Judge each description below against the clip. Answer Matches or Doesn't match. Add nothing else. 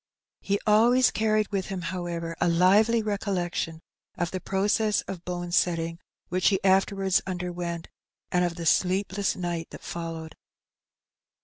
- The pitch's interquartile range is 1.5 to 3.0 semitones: Matches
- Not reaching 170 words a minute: Matches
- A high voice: Doesn't match